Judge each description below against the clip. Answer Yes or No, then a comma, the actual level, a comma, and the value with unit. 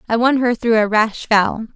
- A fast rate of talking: Yes, fast, 240 wpm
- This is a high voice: Yes, high, 225 Hz